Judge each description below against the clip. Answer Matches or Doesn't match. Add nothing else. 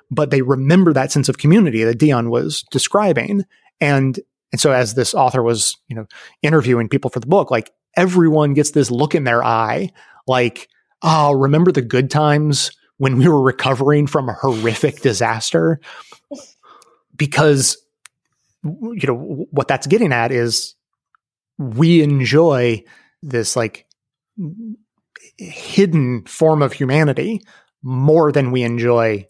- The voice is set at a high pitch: Doesn't match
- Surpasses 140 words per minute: Doesn't match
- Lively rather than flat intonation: Doesn't match